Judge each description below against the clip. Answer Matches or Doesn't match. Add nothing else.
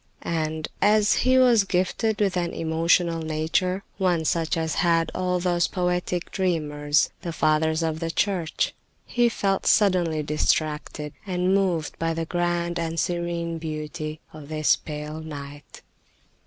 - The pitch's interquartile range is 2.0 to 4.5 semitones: Matches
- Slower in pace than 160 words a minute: Matches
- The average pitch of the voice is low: Doesn't match